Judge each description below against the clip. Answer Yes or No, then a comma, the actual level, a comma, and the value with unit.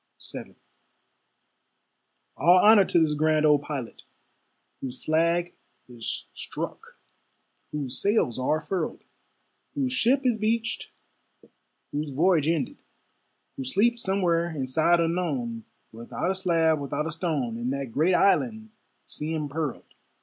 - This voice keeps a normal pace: No, slow, 120 wpm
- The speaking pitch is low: No, medium, 160 Hz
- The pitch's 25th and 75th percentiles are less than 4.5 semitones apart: No, average, 4.8 semitones